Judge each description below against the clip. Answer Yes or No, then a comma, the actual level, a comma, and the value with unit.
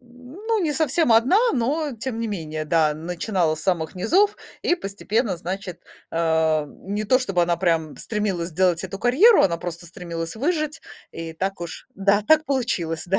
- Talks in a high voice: Yes, high, 195 Hz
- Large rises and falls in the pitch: Yes, wide, 7.0 semitones